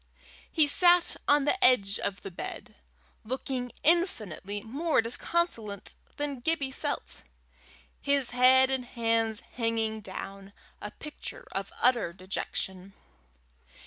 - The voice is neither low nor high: No, high, 245 Hz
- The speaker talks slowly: Yes, slow, 115 wpm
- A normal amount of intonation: No, wide, 5.7 semitones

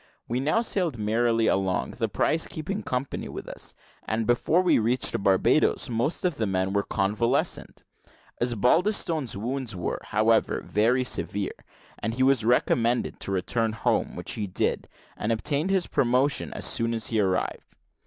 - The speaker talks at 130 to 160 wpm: Yes, average, 155 wpm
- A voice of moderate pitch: No, low, 120 Hz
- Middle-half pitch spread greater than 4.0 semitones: Yes, average, 4.4 semitones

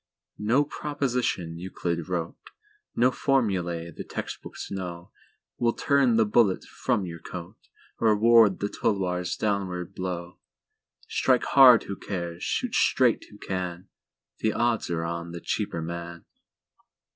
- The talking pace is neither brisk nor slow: No, slow, 110 wpm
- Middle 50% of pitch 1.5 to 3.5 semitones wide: No, average, 5.3 semitones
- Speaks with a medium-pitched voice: No, very low, 95 Hz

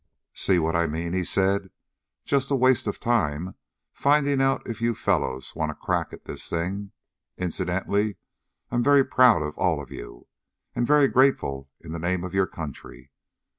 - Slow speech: No, average, 170 wpm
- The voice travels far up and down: Yes, wide, 6.9 semitones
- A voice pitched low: Yes, very low, 95 Hz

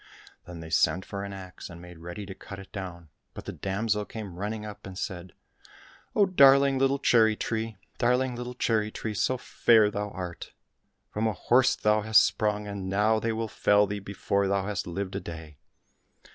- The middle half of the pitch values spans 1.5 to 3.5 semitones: Yes, average, 3.0 semitones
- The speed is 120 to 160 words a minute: No, average, 195 wpm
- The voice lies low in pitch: Yes, low, 105 Hz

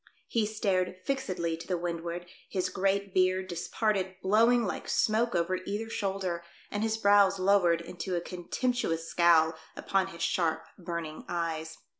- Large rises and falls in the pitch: No, average, 3.0 semitones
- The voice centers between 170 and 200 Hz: Yes, medium, 185 Hz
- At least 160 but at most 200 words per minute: No, average, 145 wpm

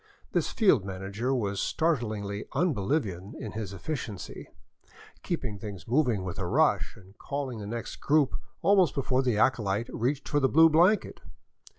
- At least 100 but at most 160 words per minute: Yes, average, 150 wpm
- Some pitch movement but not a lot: No, wide, 6.4 semitones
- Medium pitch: No, low, 120 Hz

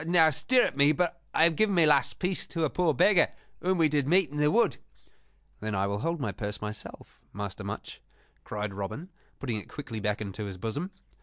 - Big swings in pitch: Yes, wide, 8.3 semitones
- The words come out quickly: Yes, fast, 210 wpm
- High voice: No, medium, 145 Hz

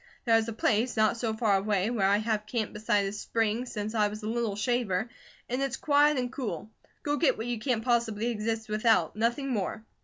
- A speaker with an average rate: No, fast, 210 wpm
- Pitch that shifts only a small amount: Yes, narrow, 2.3 semitones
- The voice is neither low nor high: No, high, 225 Hz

